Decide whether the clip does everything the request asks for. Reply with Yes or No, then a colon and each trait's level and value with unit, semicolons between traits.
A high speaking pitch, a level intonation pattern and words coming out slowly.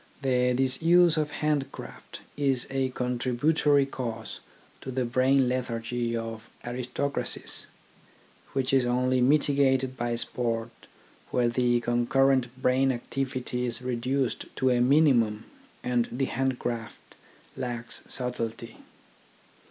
No: low, 125 Hz; narrow, 2.0 semitones; slow, 115 wpm